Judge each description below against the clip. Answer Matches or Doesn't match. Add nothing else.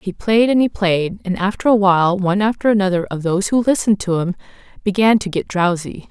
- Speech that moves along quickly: Matches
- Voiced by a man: Doesn't match